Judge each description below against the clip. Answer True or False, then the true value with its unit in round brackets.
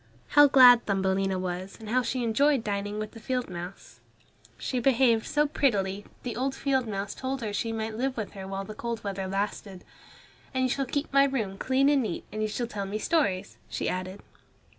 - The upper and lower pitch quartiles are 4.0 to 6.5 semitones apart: True (4.9 semitones)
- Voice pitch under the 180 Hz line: False (220 Hz)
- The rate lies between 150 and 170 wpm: False (205 wpm)